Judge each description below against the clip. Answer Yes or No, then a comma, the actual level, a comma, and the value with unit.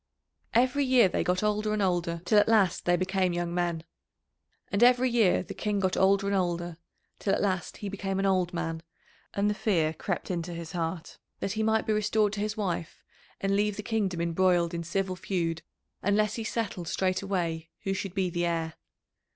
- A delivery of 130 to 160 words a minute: No, average, 195 wpm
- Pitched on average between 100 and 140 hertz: No, high, 190 Hz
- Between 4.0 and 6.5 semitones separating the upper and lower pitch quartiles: No, average, 3.3 semitones